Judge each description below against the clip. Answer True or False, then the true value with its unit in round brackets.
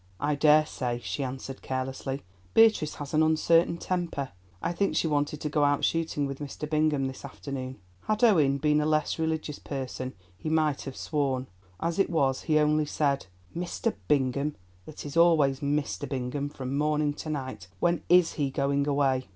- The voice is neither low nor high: True (145 Hz)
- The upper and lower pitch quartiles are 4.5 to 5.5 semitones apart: False (2.4 semitones)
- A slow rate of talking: False (170 wpm)